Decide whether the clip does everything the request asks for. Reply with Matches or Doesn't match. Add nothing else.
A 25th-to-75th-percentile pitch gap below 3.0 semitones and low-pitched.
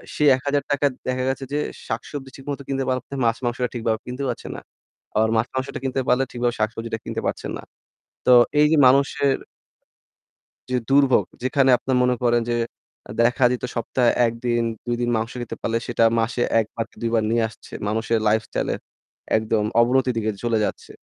Matches